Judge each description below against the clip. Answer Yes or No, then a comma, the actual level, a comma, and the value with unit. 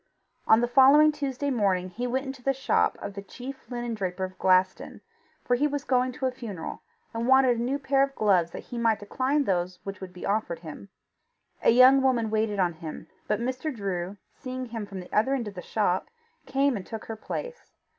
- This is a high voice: Yes, high, 235 Hz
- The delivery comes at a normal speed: No, fast, 215 wpm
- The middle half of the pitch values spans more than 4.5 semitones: Yes, average, 5.2 semitones